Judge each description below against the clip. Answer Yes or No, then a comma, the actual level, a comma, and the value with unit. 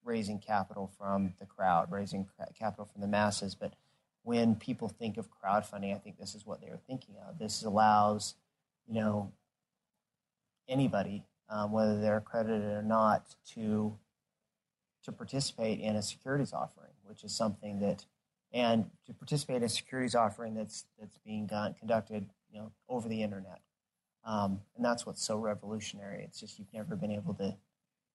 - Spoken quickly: No, average, 165 wpm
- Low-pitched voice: Yes, low, 105 Hz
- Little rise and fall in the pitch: Yes, narrow, 1.4 semitones